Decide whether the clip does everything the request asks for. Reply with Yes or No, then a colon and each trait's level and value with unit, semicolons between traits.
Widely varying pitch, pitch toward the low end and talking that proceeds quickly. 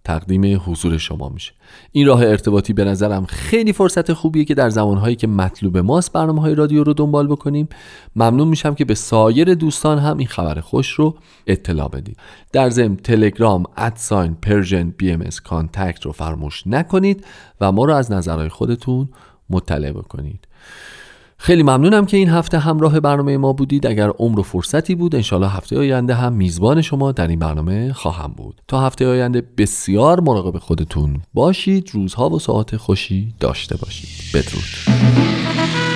Yes: wide, 8.1 semitones; low, 110 Hz; fast, 160 wpm